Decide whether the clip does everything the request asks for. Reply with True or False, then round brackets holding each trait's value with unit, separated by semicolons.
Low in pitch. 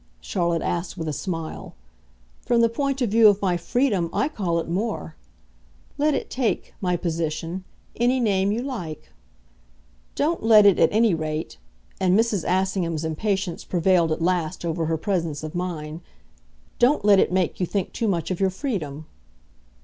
False (185 Hz)